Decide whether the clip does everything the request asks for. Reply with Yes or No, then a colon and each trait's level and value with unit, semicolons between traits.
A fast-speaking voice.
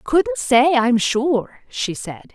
No: average, 155 wpm